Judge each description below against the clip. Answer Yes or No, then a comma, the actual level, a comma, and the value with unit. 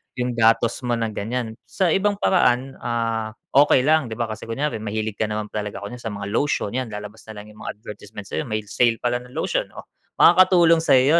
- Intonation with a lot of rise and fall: No, average, 3.7 semitones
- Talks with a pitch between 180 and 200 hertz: No, low, 115 Hz